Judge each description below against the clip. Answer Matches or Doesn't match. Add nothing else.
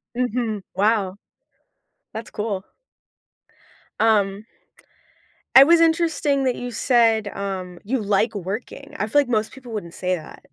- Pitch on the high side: Matches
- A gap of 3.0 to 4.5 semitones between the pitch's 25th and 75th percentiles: Matches